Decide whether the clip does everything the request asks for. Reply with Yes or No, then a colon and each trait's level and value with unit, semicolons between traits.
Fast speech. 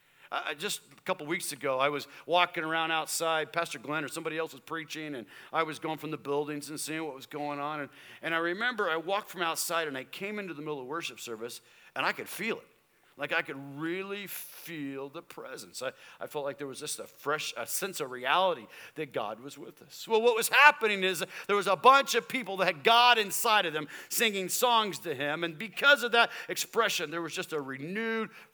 Yes: fast, 230 wpm